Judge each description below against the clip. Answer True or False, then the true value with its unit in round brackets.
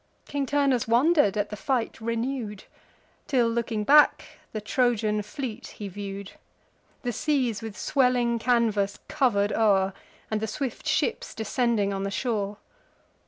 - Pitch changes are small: False (3.5 semitones)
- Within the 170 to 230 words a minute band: False (135 wpm)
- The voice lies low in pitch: False (225 Hz)